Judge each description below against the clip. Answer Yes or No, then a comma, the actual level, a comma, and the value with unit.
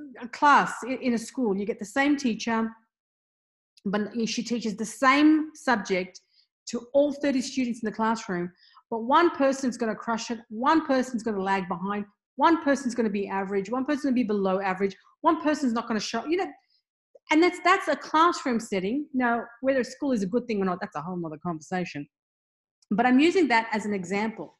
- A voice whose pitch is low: No, high, 235 Hz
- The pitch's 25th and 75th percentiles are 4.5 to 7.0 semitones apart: Yes, average, 5.1 semitones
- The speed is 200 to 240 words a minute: Yes, fast, 205 wpm